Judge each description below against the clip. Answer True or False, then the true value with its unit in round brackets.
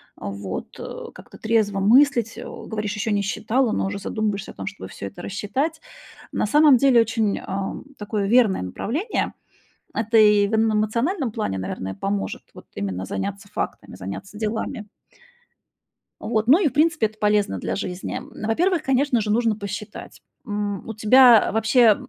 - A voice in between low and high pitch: False (215 Hz)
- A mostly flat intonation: False (3.0 semitones)